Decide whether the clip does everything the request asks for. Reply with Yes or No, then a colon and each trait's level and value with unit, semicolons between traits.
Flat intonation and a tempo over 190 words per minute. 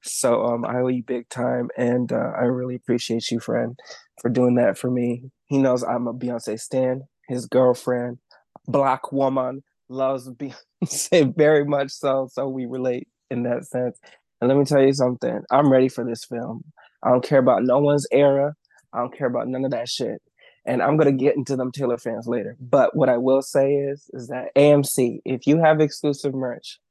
Yes: narrow, 2.1 semitones; average, 200 wpm